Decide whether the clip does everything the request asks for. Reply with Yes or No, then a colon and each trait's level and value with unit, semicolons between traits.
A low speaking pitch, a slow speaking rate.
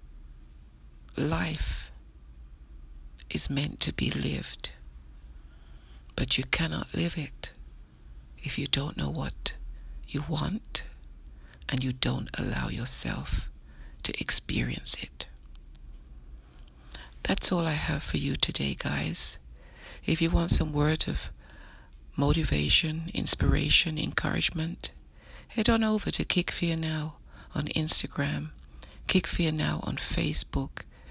Yes: very low, 65 Hz; slow, 110 wpm